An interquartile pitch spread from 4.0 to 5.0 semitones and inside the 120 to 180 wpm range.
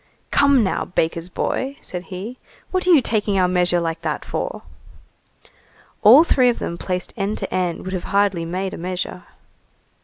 Yes: average, 4.5 semitones; average, 175 wpm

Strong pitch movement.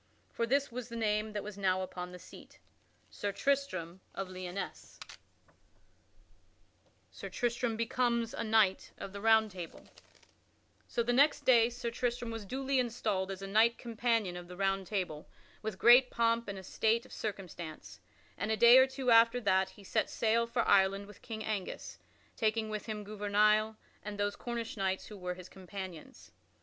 No: average, 3.3 semitones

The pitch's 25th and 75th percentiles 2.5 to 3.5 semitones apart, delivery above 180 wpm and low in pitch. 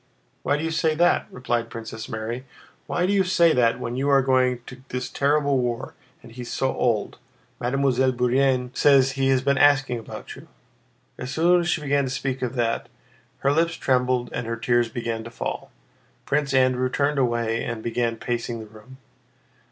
Yes: average, 2.8 semitones; average, 190 wpm; low, 130 Hz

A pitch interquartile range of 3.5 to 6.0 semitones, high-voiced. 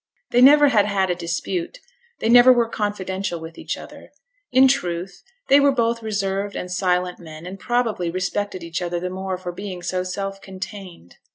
Yes: average, 4.2 semitones; high, 195 Hz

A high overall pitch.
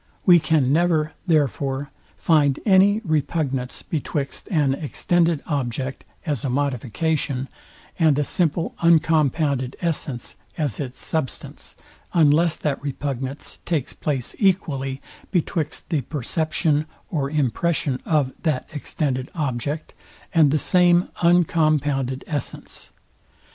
No: medium, 150 Hz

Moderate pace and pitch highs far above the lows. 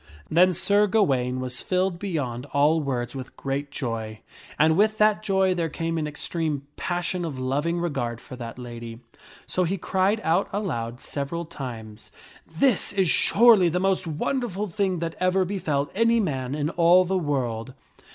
Yes: average, 170 wpm; wide, 6.2 semitones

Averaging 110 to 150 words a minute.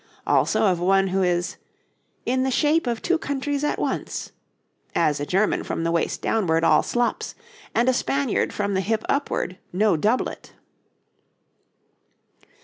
Yes: average, 145 wpm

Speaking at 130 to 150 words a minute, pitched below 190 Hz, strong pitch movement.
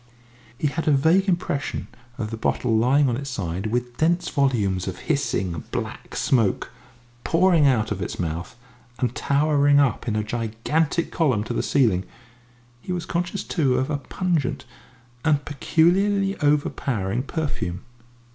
Yes: average, 145 wpm; medium, 140 Hz; wide, 6.2 semitones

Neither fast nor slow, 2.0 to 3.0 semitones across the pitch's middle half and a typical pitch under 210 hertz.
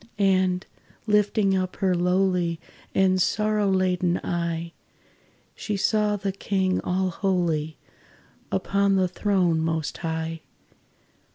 No: slow, 105 wpm; narrow, 2.4 semitones; medium, 185 Hz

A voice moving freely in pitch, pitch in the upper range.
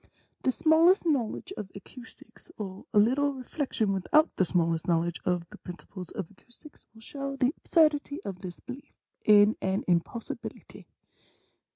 Yes: wide, 7.3 semitones; high, 220 Hz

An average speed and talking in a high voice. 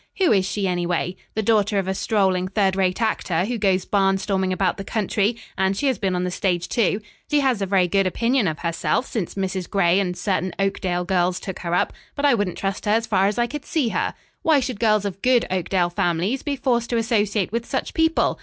No: fast, 230 wpm; high, 195 Hz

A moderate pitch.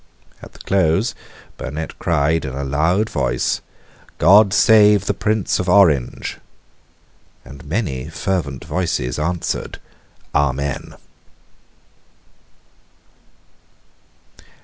No: very low, 80 Hz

